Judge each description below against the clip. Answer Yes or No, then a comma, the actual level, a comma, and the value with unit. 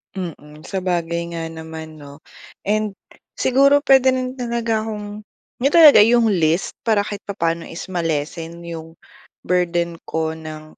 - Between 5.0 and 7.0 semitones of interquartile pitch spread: Yes, average, 5.3 semitones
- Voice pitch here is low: No, medium, 175 Hz